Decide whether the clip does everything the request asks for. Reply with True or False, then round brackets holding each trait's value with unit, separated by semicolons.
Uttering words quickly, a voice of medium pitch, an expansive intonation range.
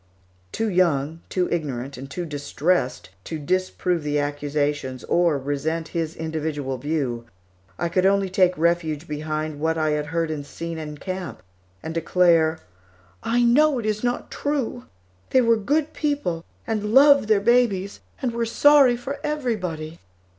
False (150 wpm; 170 Hz; 6.4 semitones)